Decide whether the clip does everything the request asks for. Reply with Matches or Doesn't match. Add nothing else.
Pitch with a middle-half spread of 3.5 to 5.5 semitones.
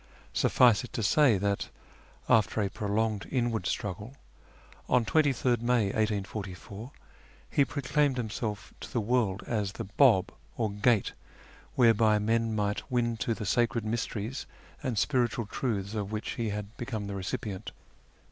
Doesn't match